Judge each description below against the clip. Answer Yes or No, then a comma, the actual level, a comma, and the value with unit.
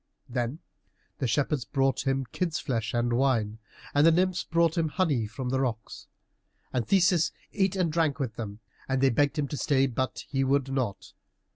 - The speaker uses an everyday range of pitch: Yes, average, 4.6 semitones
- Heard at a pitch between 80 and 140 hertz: Yes, low, 135 Hz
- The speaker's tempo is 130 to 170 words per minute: No, average, 180 wpm